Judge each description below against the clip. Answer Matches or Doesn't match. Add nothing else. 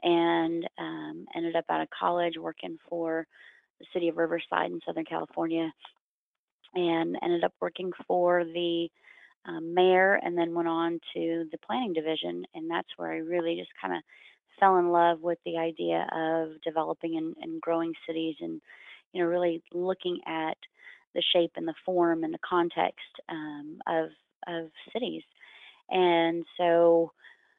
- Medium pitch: Matches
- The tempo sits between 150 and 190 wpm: Matches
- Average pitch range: Doesn't match